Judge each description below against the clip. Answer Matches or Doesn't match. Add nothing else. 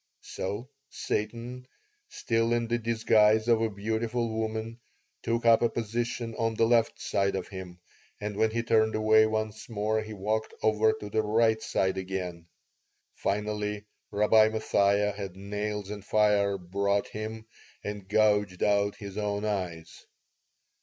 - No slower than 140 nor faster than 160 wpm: Matches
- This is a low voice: Matches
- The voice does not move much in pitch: Matches